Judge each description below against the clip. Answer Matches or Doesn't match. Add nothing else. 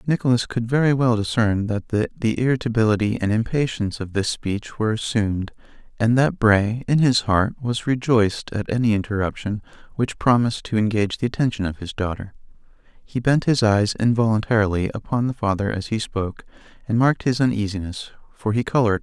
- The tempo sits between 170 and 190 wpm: Matches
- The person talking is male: Matches